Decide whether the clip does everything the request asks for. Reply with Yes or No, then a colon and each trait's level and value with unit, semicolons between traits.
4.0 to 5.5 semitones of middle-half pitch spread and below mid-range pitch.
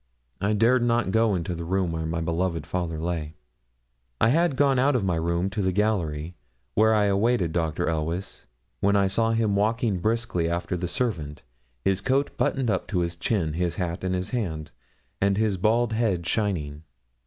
Yes: average, 4.7 semitones; very low, 95 Hz